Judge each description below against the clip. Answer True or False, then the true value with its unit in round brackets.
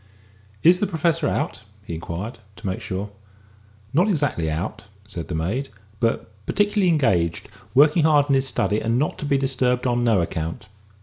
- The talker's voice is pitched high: False (125 Hz)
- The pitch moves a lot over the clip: True (7.5 semitones)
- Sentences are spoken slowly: False (175 wpm)